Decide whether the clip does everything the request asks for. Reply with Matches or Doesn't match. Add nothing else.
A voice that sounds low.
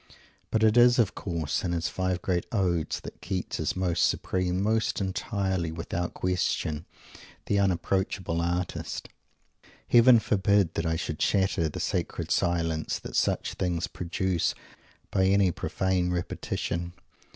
Matches